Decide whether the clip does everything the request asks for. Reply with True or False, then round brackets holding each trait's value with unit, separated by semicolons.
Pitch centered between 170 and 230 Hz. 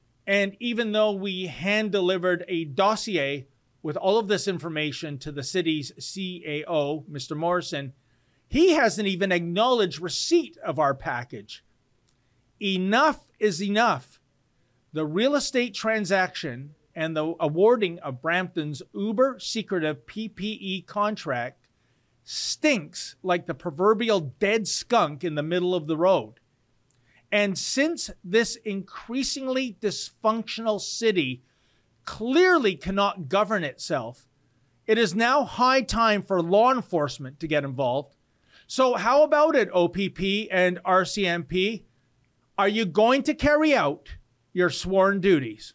True (185 Hz)